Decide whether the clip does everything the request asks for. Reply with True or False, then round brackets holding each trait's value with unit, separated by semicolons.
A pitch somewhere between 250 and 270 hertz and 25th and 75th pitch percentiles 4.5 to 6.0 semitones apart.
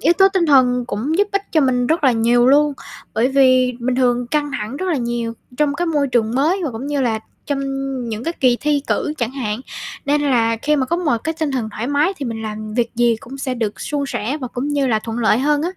False (260 Hz; 3.7 semitones)